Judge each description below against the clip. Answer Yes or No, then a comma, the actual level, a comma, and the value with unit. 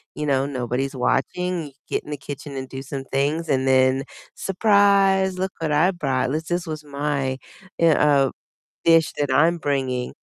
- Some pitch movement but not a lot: Yes, average, 3.9 semitones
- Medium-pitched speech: Yes, medium, 145 Hz